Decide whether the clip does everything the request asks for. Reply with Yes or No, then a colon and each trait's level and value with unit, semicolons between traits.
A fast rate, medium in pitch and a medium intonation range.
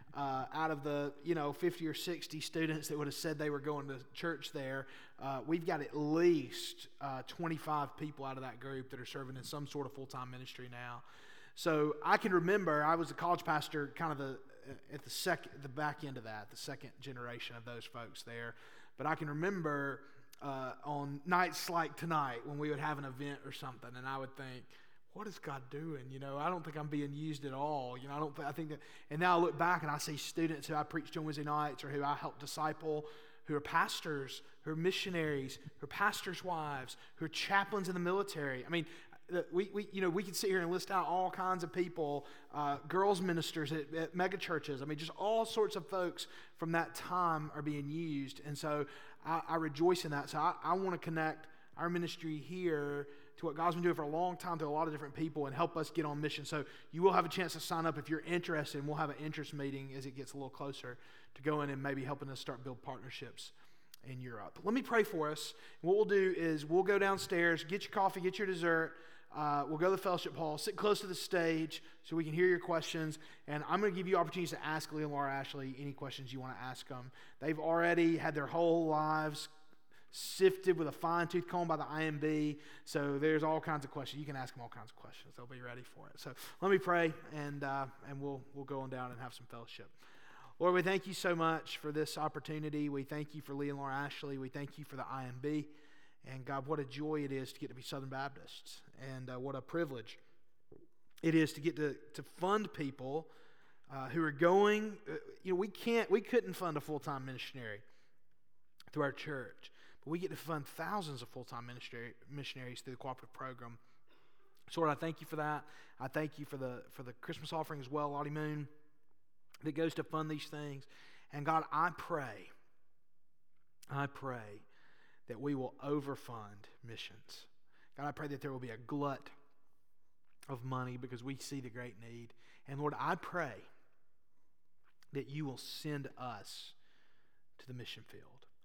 Yes: fast, 220 wpm; medium, 150 Hz; average, 3.3 semitones